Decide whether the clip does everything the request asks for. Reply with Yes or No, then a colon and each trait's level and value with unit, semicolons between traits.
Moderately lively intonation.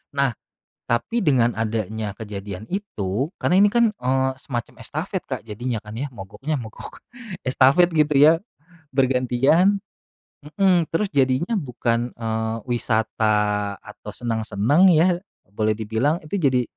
No: wide, 5.8 semitones